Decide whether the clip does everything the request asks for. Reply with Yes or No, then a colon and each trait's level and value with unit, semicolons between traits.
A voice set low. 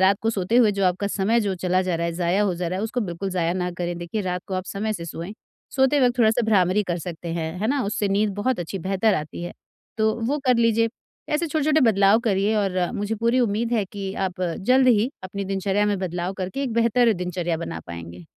No: high, 195 Hz